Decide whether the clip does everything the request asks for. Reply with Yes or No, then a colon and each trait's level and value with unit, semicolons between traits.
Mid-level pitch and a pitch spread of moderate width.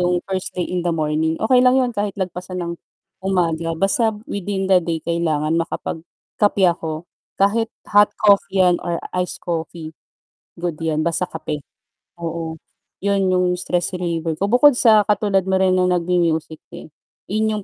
Yes: medium, 180 Hz; average, 3.1 semitones